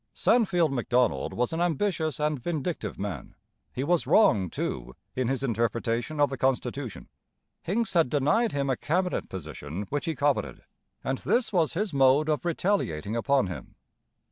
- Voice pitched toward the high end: No, medium, 140 Hz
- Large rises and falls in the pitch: Yes, wide, 6.1 semitones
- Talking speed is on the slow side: No, average, 155 wpm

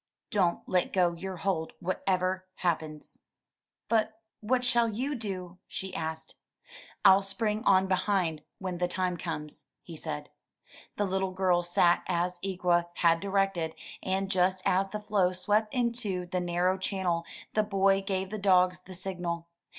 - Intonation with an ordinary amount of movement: No, narrow, 1.9 semitones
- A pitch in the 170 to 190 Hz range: Yes, medium, 185 Hz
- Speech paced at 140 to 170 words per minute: Yes, average, 150 wpm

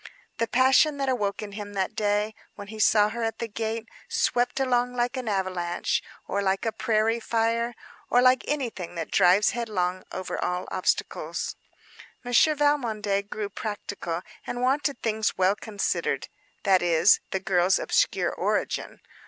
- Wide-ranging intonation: No, average, 3.7 semitones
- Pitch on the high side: Yes, high, 220 Hz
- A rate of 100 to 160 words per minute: Yes, average, 155 wpm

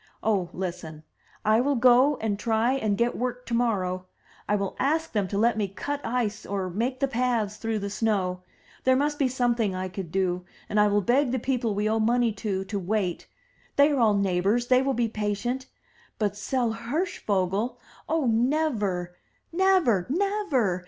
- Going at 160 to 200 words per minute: Yes, average, 180 wpm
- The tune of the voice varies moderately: Yes, average, 4.3 semitones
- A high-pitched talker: Yes, high, 225 Hz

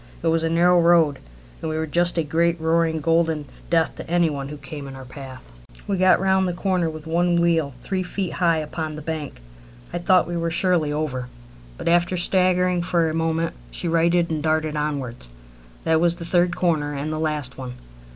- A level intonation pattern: Yes, narrow, 2.3 semitones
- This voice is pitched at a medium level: Yes, medium, 165 Hz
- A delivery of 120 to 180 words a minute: No, fast, 205 wpm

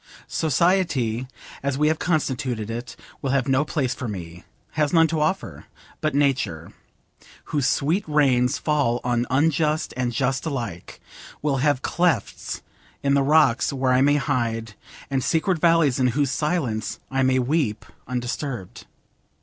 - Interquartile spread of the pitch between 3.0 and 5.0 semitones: Yes, average, 3.7 semitones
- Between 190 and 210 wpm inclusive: No, average, 145 wpm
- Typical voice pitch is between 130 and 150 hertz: Yes, low, 135 Hz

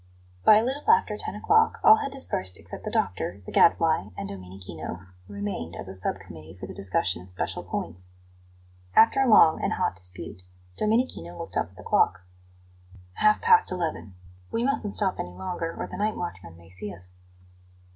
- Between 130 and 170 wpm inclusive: No, average, 185 wpm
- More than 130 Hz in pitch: No, low, 100 Hz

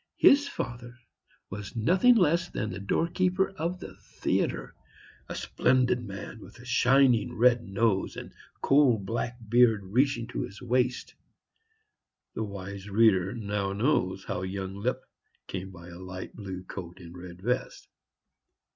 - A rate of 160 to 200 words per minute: No, average, 140 wpm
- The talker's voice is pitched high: No, low, 110 Hz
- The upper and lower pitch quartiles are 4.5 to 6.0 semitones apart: Yes, average, 4.8 semitones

